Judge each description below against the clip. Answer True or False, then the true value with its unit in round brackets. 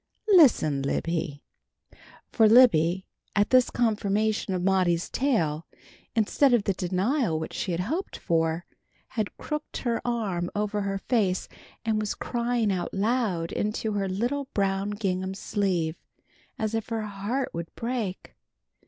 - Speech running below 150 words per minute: True (135 wpm)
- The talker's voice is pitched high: True (205 Hz)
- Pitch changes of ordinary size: True (4.2 semitones)